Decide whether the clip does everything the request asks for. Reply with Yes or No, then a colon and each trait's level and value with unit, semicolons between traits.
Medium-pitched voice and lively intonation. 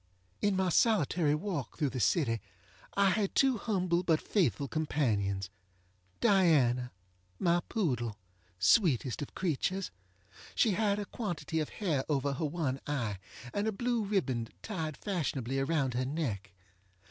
Yes: medium, 155 Hz; wide, 7.0 semitones